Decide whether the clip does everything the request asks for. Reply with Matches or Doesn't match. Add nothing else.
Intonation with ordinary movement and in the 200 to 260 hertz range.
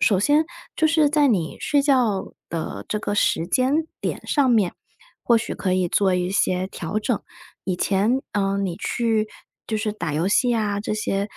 Matches